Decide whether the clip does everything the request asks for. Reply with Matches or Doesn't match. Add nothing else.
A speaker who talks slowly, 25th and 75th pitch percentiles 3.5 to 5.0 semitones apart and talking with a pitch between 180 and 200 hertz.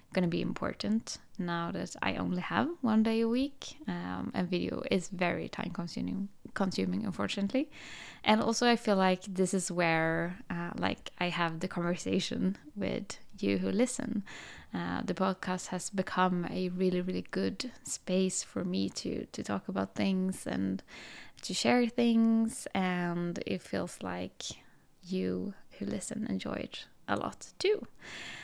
Doesn't match